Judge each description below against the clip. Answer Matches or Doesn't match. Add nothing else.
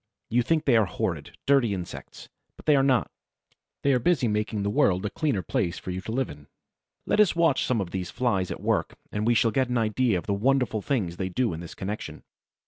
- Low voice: Matches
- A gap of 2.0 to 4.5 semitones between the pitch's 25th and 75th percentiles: Doesn't match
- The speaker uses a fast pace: Matches